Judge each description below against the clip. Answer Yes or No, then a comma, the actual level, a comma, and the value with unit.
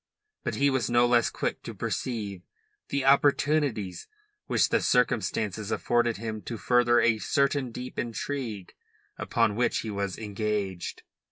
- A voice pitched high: No, low, 115 Hz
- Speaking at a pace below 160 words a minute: Yes, average, 140 wpm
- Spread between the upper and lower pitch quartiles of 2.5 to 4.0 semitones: Yes, average, 3.2 semitones